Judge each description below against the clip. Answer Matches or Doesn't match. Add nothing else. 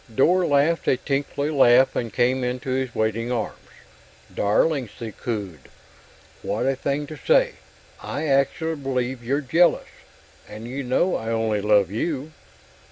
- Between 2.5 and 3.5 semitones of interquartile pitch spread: Doesn't match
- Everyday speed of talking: Matches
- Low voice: Matches